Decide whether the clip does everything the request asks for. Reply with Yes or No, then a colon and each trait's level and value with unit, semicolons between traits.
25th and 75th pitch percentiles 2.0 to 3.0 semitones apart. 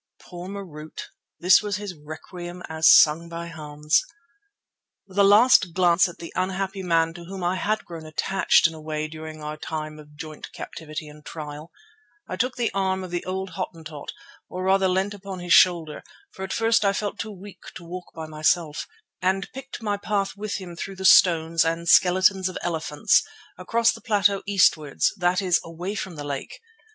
No: average, 3.4 semitones